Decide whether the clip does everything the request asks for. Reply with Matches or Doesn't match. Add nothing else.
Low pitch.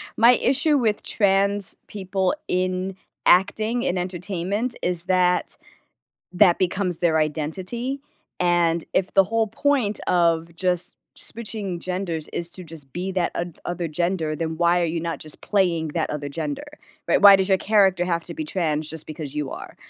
Doesn't match